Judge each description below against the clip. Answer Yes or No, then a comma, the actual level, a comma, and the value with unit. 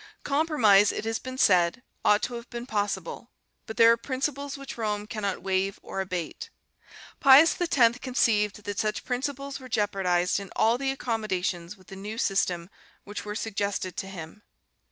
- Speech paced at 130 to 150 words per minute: No, average, 165 wpm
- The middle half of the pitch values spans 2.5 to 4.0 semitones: No, average, 4.4 semitones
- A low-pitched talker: No, high, 210 Hz